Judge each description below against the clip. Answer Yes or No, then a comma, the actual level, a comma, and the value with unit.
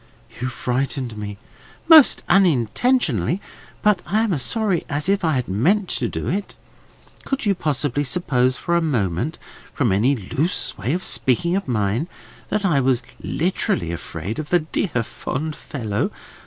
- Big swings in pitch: Yes, wide, 7.1 semitones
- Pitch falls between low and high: Yes, medium, 145 Hz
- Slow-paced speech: No, average, 155 wpm